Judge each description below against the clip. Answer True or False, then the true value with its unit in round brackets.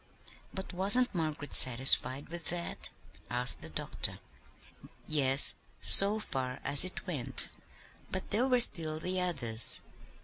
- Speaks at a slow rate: True (125 wpm)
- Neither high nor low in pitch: True (155 Hz)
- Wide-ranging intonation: True (6.0 semitones)